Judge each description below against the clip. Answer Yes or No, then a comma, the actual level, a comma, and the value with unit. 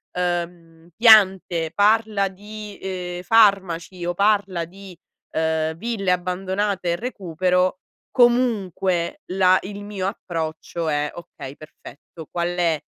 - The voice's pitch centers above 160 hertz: Yes, medium, 185 Hz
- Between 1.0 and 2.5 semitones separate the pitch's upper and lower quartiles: No, average, 2.9 semitones